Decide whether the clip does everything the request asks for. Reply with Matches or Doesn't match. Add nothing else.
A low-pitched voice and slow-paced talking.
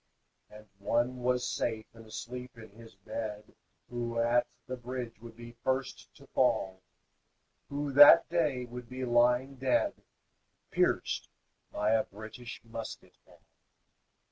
Matches